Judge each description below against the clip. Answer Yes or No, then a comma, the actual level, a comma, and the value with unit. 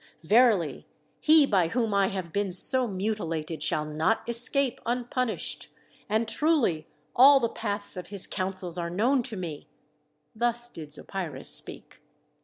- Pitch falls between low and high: No, high, 205 Hz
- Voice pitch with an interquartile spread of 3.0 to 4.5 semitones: No, wide, 5.4 semitones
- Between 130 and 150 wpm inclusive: Yes, average, 140 wpm